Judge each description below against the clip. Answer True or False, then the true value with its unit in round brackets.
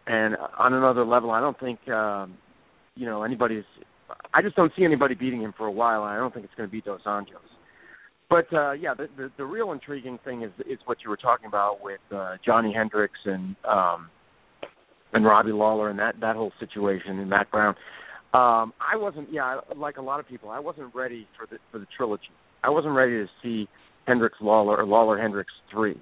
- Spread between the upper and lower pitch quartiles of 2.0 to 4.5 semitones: True (3.6 semitones)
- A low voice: True (115 Hz)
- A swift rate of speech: True (210 wpm)